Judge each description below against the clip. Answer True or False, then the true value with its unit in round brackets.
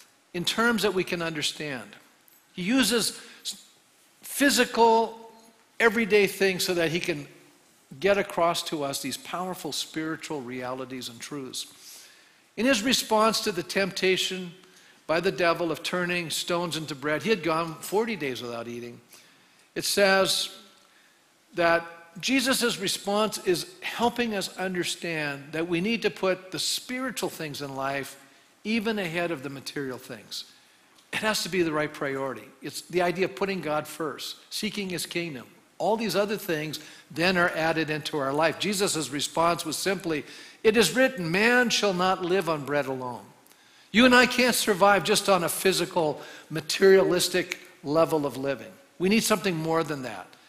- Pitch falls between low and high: True (175 Hz)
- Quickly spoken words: False (155 wpm)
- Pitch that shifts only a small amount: False (4.7 semitones)